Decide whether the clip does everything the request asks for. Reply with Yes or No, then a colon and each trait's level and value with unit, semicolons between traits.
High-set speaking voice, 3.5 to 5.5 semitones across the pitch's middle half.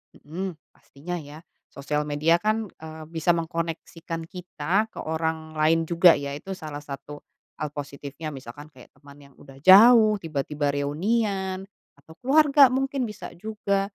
No: medium, 165 Hz; average, 4.8 semitones